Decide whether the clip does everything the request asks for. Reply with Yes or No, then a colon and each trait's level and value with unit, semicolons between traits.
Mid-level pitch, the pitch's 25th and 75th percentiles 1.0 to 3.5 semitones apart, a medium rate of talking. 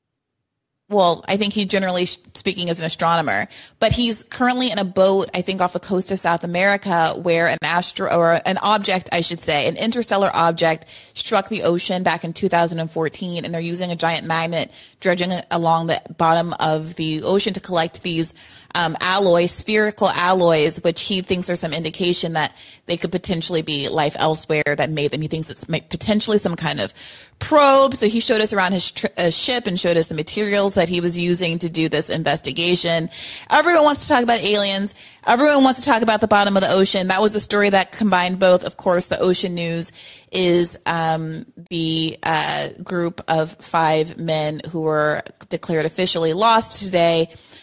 Yes: medium, 175 Hz; average, 3.0 semitones; average, 190 wpm